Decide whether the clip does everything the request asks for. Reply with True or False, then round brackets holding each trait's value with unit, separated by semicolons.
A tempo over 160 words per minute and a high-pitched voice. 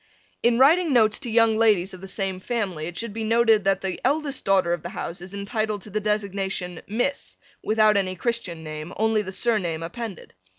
True (200 wpm; 210 Hz)